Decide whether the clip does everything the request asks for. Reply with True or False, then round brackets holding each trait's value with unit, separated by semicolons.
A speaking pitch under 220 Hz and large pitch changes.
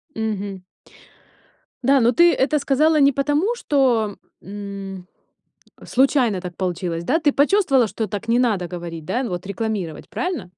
False (225 Hz; 6.6 semitones)